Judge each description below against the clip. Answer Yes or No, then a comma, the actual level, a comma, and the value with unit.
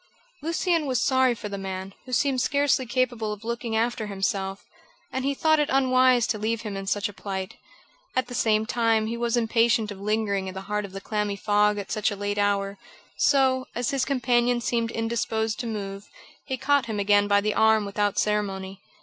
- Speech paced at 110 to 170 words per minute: No, average, 200 wpm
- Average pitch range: Yes, average, 3.4 semitones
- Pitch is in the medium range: No, high, 220 Hz